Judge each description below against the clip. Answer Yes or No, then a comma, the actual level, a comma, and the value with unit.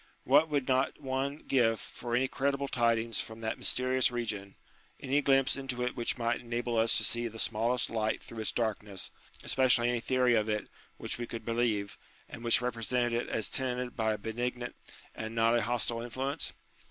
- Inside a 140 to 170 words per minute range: No, average, 185 wpm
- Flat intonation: Yes, narrow, 2.1 semitones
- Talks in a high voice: No, low, 120 Hz